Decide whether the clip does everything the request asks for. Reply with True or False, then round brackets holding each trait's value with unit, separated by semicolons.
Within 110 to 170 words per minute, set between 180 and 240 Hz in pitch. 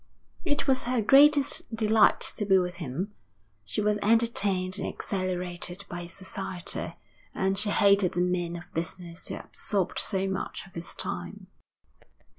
True (150 wpm; 190 Hz)